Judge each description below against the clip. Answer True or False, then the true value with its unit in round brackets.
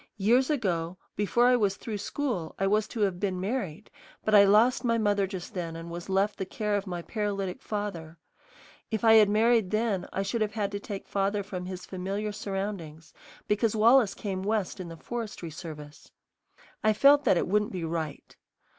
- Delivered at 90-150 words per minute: False (190 wpm)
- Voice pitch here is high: True (200 Hz)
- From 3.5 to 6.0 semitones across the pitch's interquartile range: False (2.9 semitones)